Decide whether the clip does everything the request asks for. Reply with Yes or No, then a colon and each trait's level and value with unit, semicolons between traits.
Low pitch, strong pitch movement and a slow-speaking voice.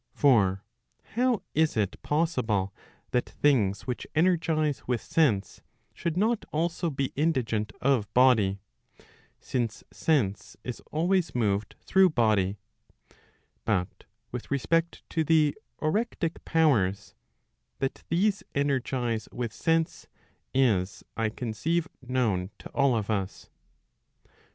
Yes: low, 130 Hz; wide, 6.9 semitones; slow, 110 wpm